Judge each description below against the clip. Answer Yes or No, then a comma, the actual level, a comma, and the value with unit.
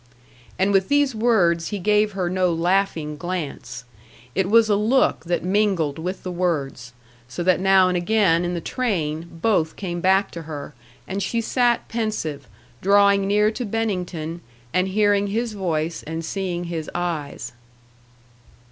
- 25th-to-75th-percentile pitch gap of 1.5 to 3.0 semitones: No, average, 3.7 semitones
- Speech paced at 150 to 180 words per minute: Yes, average, 155 wpm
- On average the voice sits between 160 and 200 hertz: Yes, medium, 185 Hz